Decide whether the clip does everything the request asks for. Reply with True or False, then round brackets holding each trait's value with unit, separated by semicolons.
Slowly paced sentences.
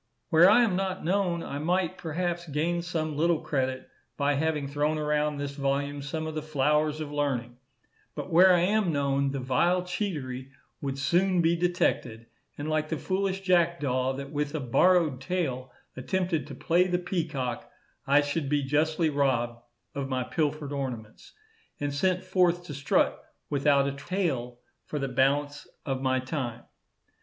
False (165 wpm)